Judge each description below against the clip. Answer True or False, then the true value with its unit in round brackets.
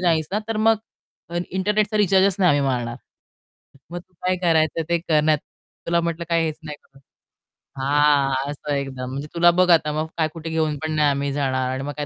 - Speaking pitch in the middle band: True (155 Hz)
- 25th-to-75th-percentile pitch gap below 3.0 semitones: False (3.4 semitones)